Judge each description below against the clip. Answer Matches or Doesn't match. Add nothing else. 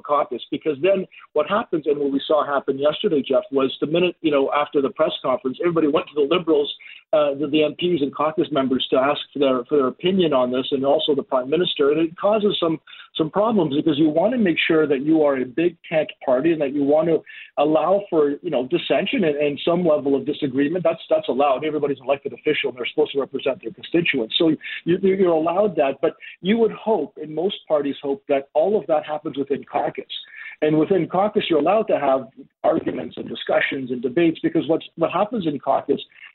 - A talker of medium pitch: Matches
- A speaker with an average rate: Doesn't match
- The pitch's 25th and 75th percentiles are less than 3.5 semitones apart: Doesn't match